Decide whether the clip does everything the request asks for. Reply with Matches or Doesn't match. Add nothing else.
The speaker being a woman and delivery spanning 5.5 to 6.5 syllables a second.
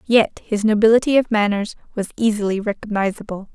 Matches